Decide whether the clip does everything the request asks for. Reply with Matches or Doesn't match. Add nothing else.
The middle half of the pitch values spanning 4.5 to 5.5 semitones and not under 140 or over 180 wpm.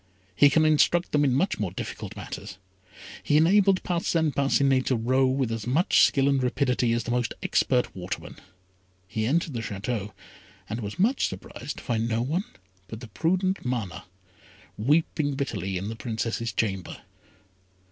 Matches